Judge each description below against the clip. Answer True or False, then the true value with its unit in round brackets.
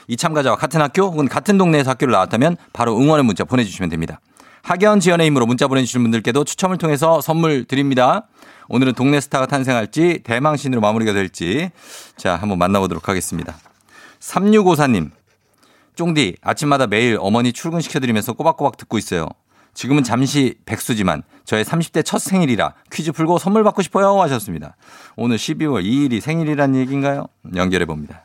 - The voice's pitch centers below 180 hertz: True (140 Hz)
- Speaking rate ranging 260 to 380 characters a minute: False (400 characters per minute)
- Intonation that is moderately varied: False (5.8 semitones)